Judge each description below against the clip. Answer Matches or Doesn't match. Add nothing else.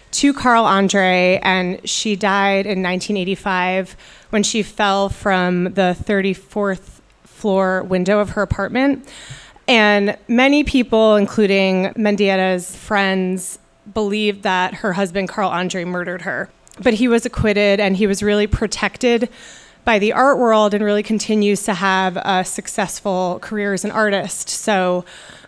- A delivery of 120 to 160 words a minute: Matches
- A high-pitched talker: Matches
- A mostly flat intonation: Matches